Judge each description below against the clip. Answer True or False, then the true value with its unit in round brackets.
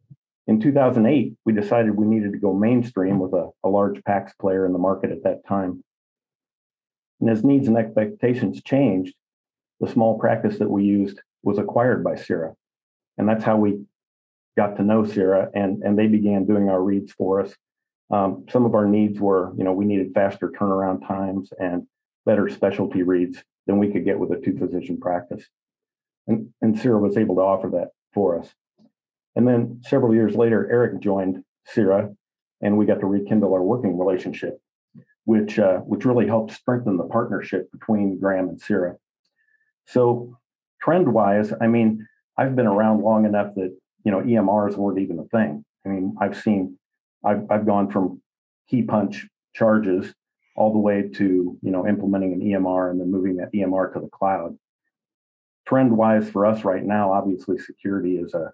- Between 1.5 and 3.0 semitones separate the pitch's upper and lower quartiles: True (2.5 semitones)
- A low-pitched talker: True (100 Hz)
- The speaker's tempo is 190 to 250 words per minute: False (175 wpm)